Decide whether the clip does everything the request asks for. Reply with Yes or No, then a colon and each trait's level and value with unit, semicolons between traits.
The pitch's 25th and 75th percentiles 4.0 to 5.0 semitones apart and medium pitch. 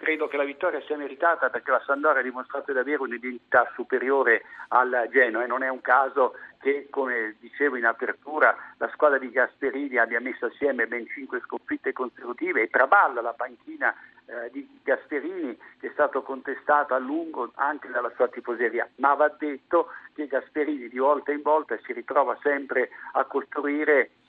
Yes: average, 4.5 semitones; medium, 145 Hz